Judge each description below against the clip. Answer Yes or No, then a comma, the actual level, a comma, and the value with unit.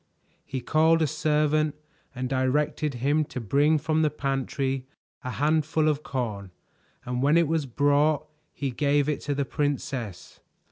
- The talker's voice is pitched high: No, medium, 145 Hz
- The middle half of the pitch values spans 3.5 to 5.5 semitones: No, narrow, 2.6 semitones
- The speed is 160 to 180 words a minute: No, average, 150 wpm